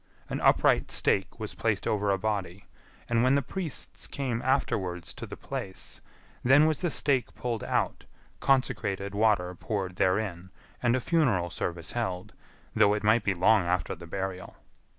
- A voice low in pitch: Yes, low, 105 Hz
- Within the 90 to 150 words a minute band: No, average, 160 wpm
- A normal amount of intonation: Yes, average, 4.6 semitones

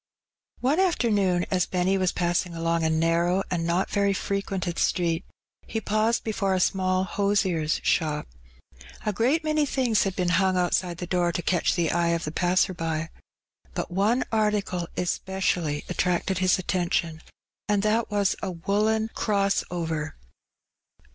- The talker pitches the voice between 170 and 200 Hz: Yes, medium, 185 Hz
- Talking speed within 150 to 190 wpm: Yes, average, 155 wpm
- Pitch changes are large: No, average, 3.0 semitones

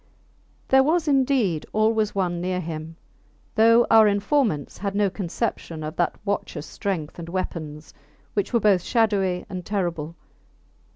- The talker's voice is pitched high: Yes, high, 195 Hz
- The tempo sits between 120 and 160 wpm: Yes, slow, 135 wpm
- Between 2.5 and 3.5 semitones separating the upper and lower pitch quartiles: No, average, 4.6 semitones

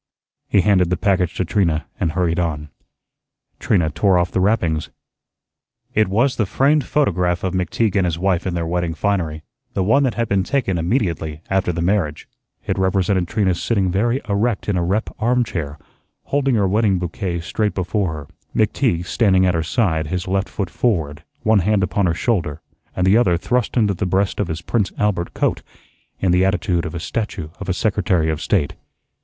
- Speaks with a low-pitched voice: Yes, very low, 95 Hz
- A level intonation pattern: No, average, 3.4 semitones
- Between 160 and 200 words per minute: Yes, average, 190 wpm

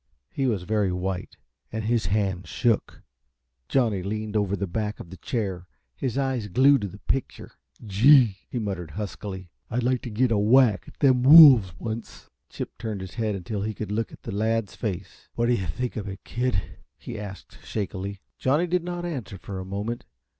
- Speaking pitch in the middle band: No, low, 105 Hz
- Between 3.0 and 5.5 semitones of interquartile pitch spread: Yes, average, 4.1 semitones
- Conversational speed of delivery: Yes, average, 190 wpm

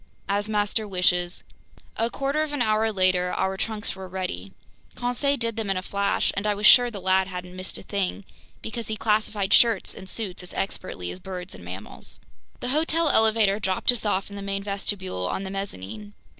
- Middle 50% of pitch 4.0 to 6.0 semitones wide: No, average, 2.9 semitones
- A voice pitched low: No, high, 200 Hz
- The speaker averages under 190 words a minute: No, average, 200 wpm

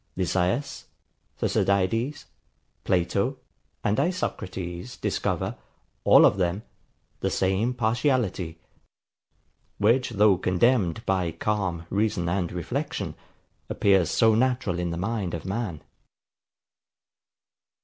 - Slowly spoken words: Yes, slow, 95 wpm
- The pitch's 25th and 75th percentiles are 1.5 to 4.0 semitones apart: No, average, 4.6 semitones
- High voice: No, low, 100 Hz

